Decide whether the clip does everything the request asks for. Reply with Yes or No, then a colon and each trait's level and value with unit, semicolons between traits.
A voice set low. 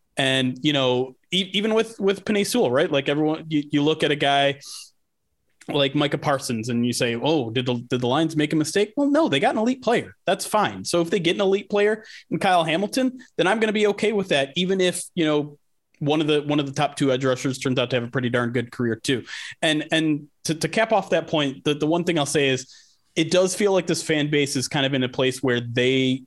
No: medium, 150 Hz